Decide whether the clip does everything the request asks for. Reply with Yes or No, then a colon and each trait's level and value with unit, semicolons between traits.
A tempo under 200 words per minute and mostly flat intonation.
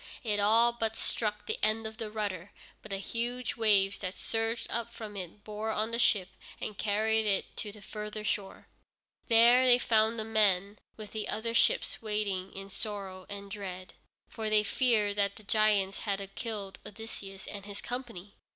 Yes: average, 180 wpm; narrow, 1.9 semitones